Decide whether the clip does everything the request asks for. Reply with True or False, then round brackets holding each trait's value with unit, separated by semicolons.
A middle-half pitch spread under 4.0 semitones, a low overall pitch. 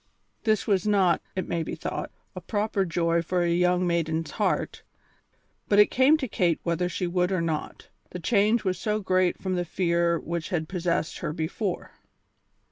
False (2.7 semitones; 180 Hz)